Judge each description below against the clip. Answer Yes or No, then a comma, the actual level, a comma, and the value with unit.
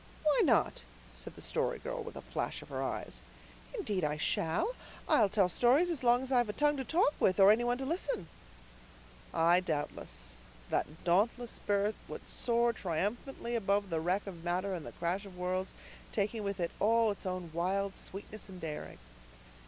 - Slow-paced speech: No, average, 185 wpm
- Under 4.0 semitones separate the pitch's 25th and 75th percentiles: No, average, 5.0 semitones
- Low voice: No, high, 200 Hz